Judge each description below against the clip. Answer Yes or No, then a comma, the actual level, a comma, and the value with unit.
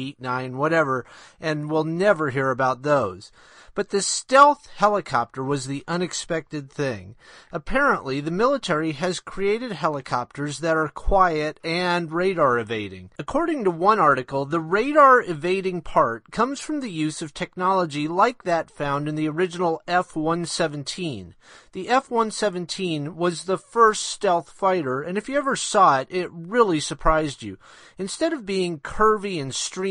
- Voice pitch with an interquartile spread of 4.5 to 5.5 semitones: Yes, average, 5.1 semitones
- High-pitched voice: No, medium, 170 Hz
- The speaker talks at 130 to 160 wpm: Yes, average, 150 wpm